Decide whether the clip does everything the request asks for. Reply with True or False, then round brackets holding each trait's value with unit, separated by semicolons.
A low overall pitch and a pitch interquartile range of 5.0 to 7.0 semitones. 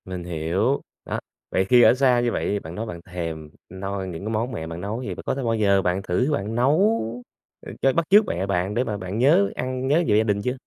True (105 Hz; 5.5 semitones)